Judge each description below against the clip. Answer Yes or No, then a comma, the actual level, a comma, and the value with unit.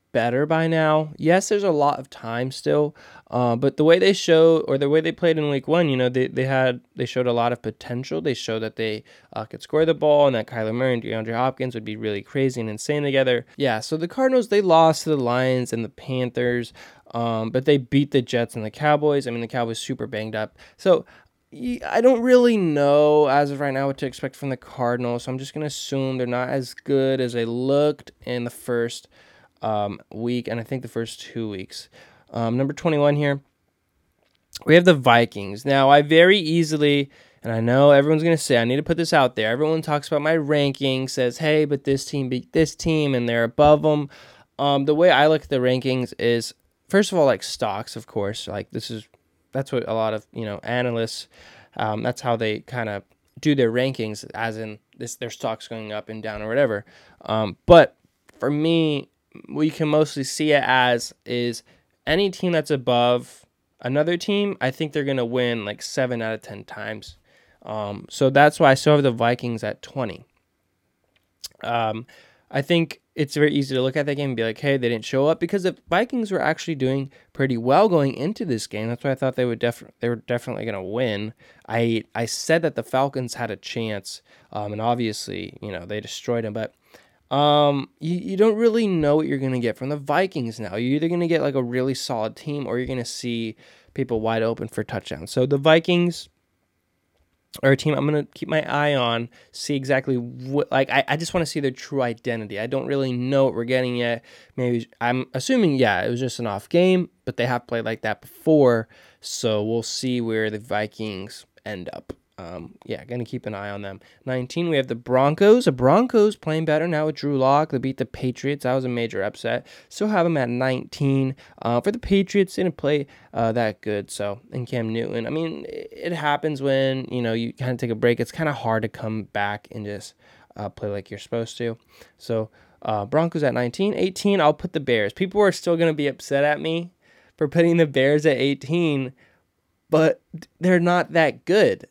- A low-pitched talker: Yes, low, 130 Hz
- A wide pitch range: No, average, 4.6 semitones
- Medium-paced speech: No, fast, 215 wpm